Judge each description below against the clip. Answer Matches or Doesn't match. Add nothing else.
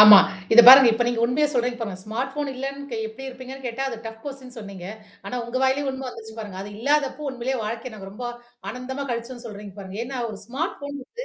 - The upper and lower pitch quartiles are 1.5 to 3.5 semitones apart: Matches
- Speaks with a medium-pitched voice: Doesn't match